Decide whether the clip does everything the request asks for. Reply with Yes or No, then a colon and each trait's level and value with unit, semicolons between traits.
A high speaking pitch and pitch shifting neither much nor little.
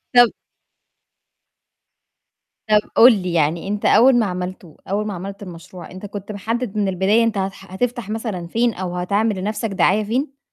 Yes: high, 200 Hz; average, 3.3 semitones